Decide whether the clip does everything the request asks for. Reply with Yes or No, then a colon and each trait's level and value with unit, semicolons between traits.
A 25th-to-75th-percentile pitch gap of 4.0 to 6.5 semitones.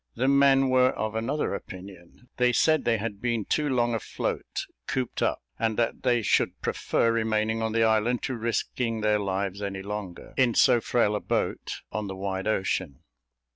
No: average, 3.3 semitones